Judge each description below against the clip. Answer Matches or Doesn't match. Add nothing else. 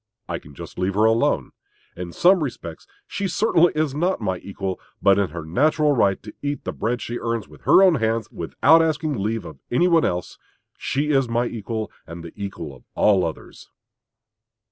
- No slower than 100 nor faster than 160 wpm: Doesn't match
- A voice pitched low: Matches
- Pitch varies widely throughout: Matches